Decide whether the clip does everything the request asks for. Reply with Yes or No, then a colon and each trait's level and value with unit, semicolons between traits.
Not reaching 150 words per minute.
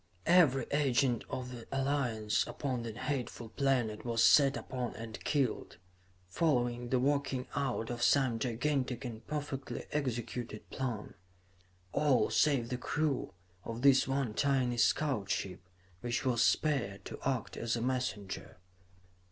Yes: slow, 135 wpm